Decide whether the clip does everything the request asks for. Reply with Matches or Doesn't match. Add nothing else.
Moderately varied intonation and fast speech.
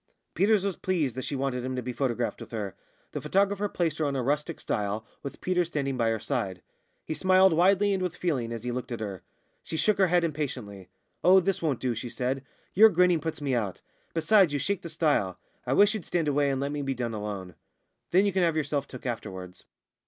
Doesn't match